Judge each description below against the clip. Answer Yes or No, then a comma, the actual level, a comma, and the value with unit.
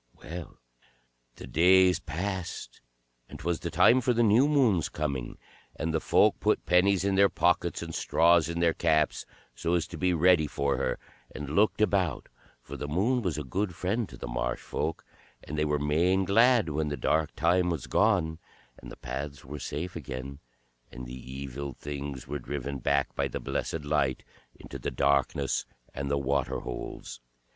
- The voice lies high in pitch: No, very low, 80 Hz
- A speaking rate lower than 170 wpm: No, average, 180 wpm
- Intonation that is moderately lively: Yes, average, 4.5 semitones